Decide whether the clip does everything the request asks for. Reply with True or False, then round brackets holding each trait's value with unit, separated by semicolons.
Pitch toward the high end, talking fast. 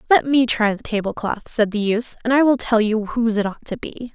True (230 Hz; 275 wpm)